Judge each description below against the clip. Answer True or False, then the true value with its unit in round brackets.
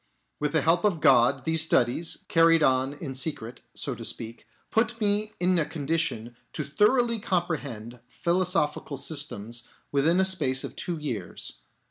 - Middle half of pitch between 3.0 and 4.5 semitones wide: False (5.1 semitones)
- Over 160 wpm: False (150 wpm)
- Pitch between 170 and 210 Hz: False (155 Hz)